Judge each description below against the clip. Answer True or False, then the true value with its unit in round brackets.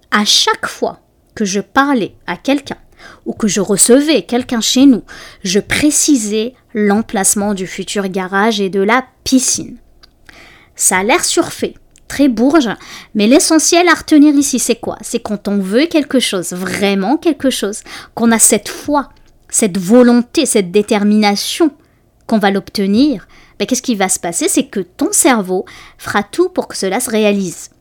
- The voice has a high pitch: True (230 Hz)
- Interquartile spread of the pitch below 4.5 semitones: False (5.6 semitones)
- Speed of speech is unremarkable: True (160 wpm)